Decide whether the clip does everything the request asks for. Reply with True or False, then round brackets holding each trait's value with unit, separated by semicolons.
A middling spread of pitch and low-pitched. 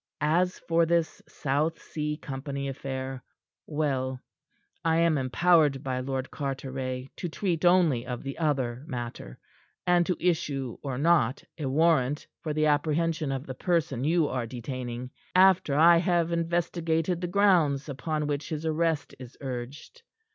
False (4.0 semitones; 150 Hz)